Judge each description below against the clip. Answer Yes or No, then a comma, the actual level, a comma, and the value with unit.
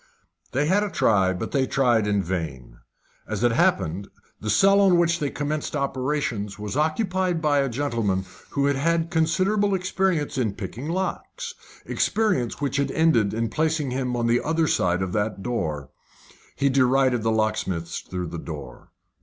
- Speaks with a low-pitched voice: Yes, low, 130 Hz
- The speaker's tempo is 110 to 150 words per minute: No, average, 165 wpm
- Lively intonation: Yes, wide, 7.5 semitones